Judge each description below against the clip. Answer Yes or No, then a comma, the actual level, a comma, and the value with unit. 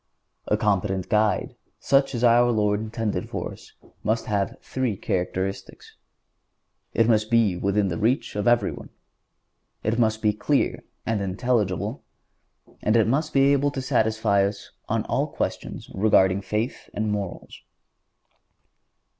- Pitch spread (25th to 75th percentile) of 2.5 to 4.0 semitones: Yes, average, 2.8 semitones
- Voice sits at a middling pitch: No, low, 110 Hz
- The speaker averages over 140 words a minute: No, slow, 135 wpm